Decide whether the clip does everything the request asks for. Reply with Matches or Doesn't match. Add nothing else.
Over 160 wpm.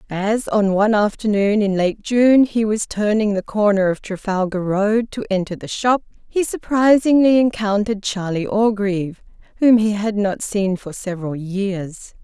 Doesn't match